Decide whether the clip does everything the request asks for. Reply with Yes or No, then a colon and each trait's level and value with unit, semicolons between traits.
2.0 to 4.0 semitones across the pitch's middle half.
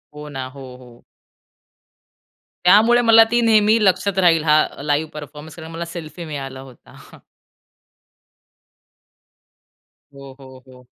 No: wide, 5.4 semitones